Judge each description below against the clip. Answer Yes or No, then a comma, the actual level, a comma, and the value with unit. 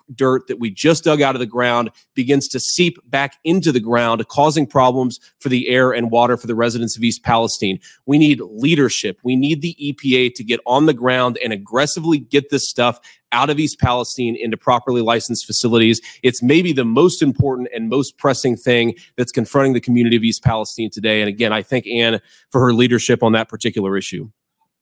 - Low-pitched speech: Yes, low, 125 Hz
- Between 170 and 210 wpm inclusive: Yes, average, 200 wpm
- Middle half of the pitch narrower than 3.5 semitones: Yes, average, 2.9 semitones